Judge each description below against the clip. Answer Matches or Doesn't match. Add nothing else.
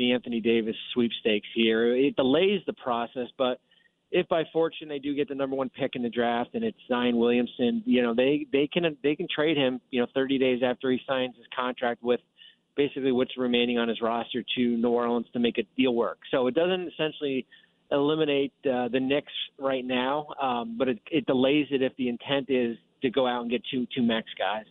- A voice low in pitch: Matches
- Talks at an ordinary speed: Doesn't match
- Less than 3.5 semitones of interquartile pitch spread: Matches